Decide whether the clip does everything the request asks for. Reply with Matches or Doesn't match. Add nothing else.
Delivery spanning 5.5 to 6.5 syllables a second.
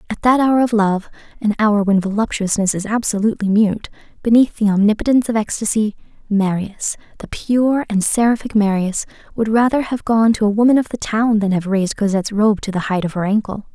Matches